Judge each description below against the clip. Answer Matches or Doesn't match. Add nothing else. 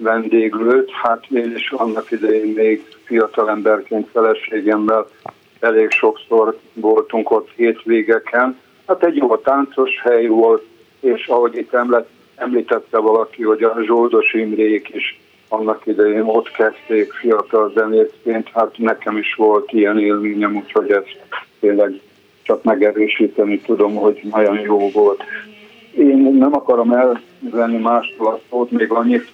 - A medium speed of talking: Matches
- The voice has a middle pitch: Doesn't match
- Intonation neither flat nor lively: Doesn't match